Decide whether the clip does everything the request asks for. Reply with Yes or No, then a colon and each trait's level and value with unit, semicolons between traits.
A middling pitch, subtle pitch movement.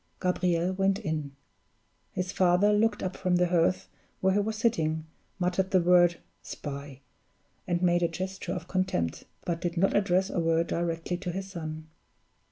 Yes: medium, 180 Hz; narrow, 2.2 semitones